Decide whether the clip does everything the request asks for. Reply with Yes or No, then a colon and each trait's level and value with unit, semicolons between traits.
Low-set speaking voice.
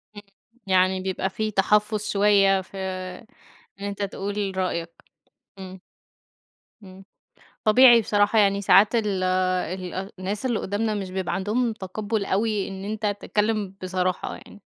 No: high, 200 Hz